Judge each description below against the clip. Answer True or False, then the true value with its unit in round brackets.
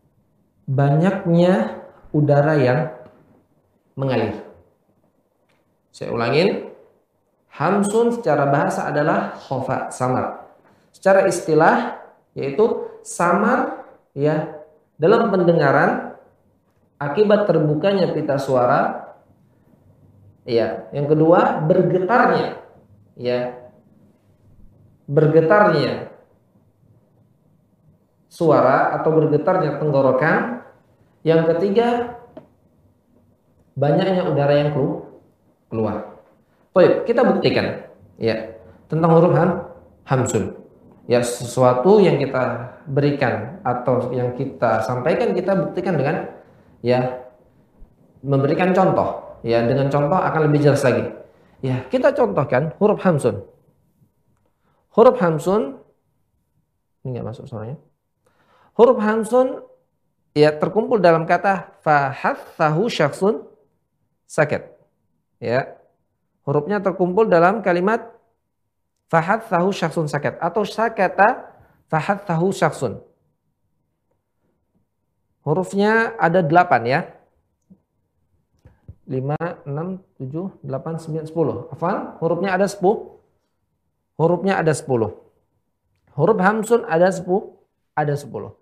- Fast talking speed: False (85 wpm)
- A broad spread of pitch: True (7.0 semitones)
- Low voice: False (155 Hz)